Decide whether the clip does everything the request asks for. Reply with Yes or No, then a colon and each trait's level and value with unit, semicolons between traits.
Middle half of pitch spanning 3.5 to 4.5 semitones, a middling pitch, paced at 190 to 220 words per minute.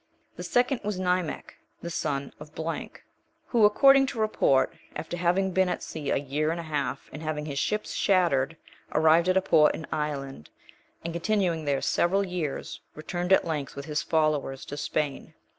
No: average, 3.8 semitones; medium, 160 Hz; average, 175 wpm